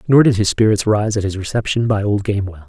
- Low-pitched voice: Yes, low, 105 Hz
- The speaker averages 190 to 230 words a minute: No, fast, 245 wpm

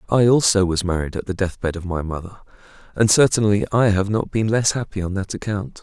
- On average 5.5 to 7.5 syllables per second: Yes, 5.8 syllables/s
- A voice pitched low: Yes, low, 100 Hz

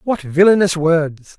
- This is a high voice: No, medium, 170 Hz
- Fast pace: No, slow, 130 wpm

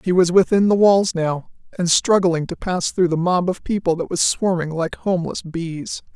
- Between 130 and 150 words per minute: No, fast, 205 wpm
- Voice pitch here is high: No, medium, 175 Hz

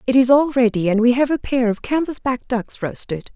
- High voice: Yes, high, 245 Hz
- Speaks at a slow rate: No, fast, 235 wpm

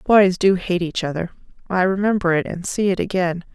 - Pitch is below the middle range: No, medium, 185 Hz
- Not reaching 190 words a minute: No, fast, 205 wpm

